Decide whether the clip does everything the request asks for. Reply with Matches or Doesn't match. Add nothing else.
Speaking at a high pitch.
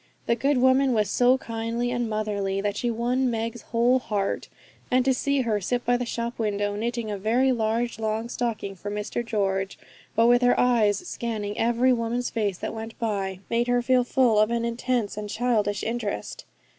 Matches